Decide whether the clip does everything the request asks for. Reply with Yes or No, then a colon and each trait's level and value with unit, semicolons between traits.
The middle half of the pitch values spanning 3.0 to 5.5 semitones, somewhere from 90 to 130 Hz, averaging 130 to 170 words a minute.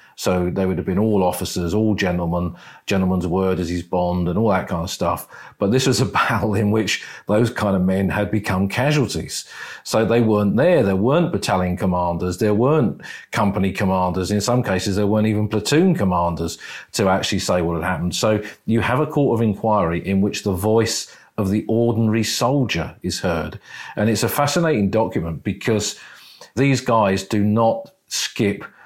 No: average, 3.4 semitones; low, 105 Hz; average, 185 wpm